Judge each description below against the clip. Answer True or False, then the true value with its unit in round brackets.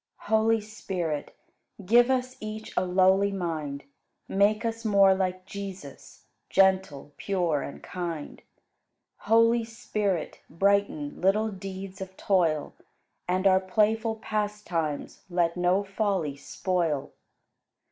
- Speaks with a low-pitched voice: False (190 Hz)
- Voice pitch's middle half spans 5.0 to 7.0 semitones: False (3.3 semitones)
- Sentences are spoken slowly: True (110 wpm)